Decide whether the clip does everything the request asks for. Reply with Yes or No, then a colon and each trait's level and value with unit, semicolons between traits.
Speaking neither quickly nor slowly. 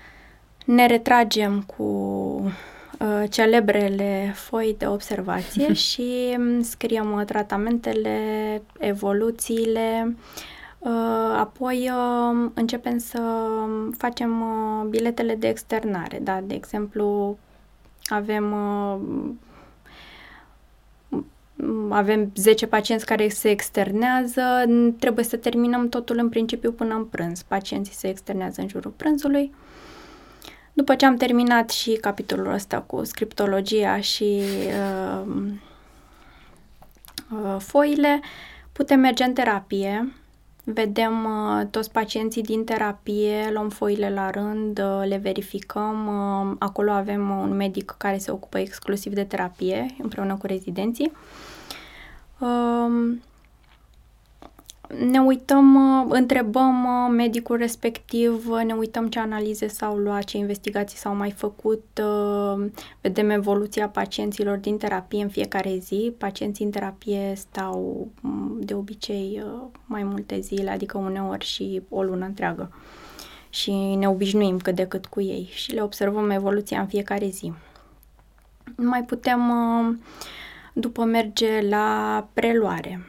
No: slow, 110 wpm